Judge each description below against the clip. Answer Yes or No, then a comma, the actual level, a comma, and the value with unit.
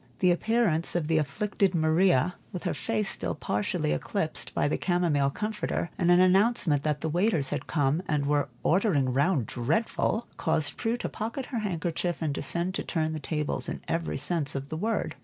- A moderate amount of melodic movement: Yes, average, 4.8 semitones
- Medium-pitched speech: Yes, medium, 165 Hz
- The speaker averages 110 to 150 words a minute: No, average, 185 wpm